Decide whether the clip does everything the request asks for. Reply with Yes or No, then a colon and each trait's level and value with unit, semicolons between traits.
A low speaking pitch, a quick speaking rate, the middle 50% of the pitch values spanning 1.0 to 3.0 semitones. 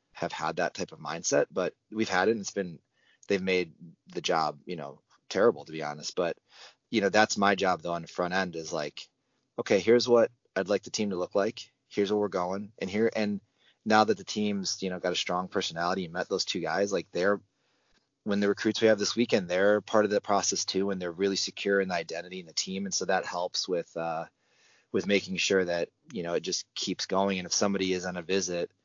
Yes: very low, 95 Hz; fast, 240 wpm; narrow, 2.4 semitones